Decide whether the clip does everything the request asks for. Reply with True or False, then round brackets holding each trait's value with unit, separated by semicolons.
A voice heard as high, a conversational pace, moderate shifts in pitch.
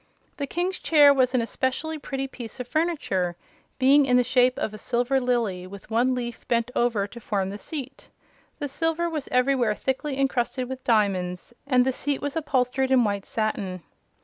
True (250 Hz; 180 wpm; 3.5 semitones)